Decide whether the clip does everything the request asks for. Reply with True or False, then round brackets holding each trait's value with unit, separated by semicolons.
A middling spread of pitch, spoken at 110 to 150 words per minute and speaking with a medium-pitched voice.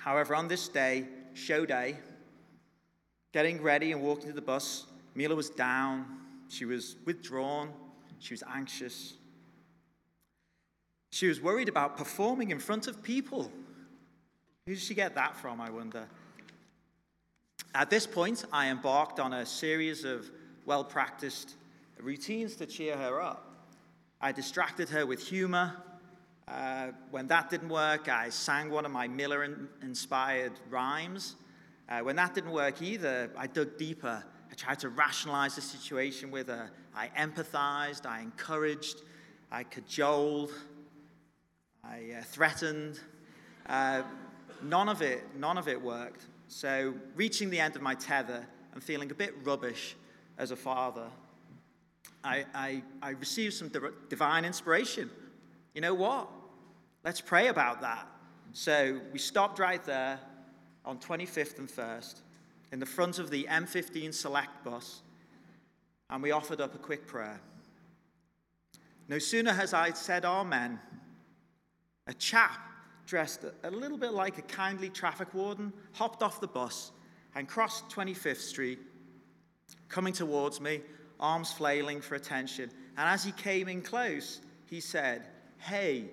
True (4.1 semitones; 140 wpm; 145 Hz)